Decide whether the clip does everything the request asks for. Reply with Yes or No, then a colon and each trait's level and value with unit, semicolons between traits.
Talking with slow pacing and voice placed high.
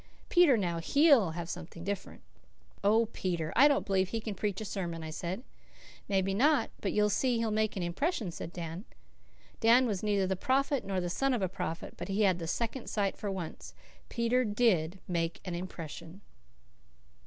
No: average, 185 wpm; high, 195 Hz